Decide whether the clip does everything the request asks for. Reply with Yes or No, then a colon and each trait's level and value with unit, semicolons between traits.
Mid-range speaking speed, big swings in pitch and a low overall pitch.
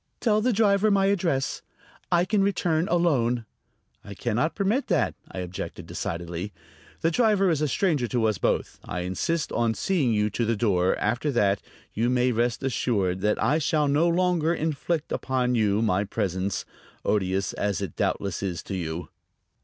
Yes: average, 170 wpm; wide, 8.9 semitones; low, 125 Hz